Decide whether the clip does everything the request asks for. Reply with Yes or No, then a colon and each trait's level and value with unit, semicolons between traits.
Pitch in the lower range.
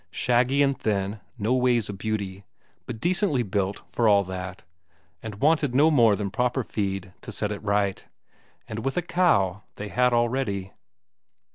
Yes: low, 110 Hz